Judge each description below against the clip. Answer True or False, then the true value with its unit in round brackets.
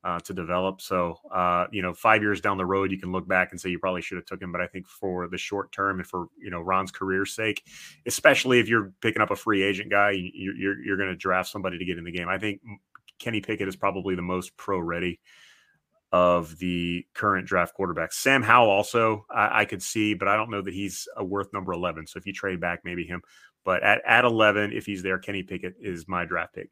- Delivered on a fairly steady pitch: True (2.0 semitones)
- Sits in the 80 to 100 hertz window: True (95 Hz)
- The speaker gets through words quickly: True (245 wpm)